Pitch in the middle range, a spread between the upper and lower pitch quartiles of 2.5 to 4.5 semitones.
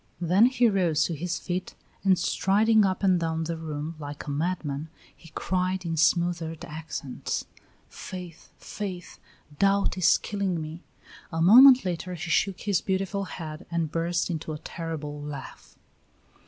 Yes: medium, 170 Hz; average, 2.8 semitones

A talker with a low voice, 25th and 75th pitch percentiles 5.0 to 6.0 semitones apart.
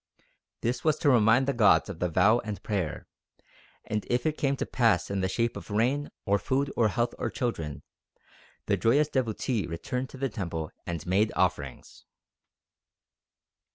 Yes: low, 110 Hz; wide, 5.6 semitones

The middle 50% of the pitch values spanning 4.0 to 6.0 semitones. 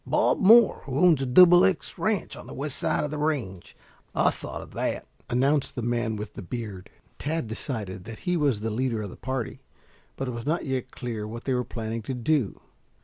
Yes: average, 5.1 semitones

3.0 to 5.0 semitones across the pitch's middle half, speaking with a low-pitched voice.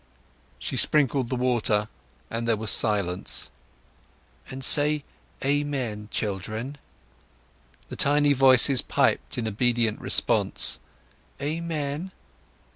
Yes: average, 4.7 semitones; low, 130 Hz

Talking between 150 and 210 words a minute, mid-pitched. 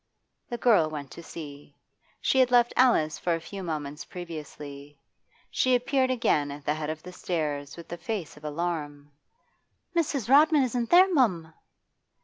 Yes: average, 160 wpm; medium, 170 Hz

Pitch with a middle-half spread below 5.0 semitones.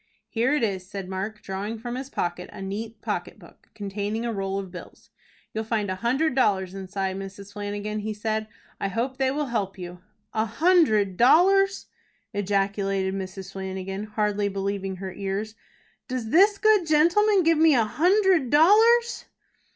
No: wide, 5.6 semitones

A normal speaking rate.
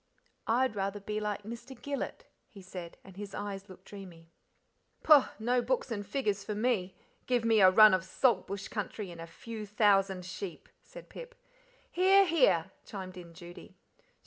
Yes: average, 170 wpm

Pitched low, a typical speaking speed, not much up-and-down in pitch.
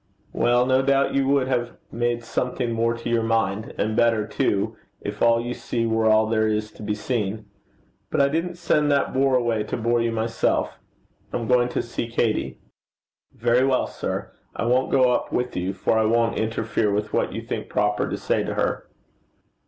Yes: low, 115 Hz; average, 195 wpm; narrow, 2.3 semitones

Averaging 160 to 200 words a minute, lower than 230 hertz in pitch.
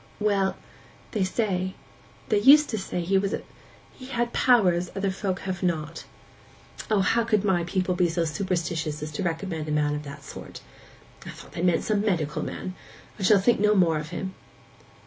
Yes: average, 175 wpm; medium, 185 Hz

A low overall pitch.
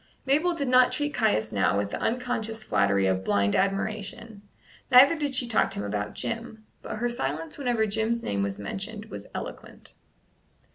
No: high, 220 Hz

